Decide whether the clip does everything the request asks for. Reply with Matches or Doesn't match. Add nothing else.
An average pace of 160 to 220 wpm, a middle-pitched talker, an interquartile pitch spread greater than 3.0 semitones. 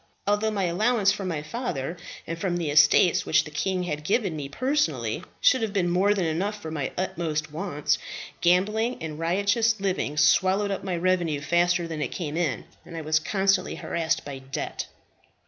Matches